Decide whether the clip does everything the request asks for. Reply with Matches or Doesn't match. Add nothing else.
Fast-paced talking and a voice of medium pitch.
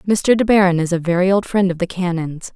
Matches